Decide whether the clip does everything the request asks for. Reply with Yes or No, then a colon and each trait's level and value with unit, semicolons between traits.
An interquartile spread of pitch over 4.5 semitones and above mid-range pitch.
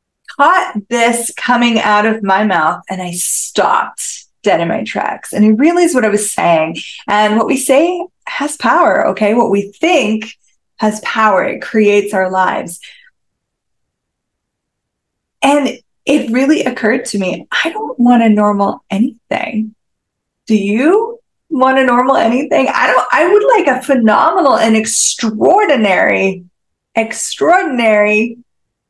Yes: average, 5.0 semitones; high, 230 Hz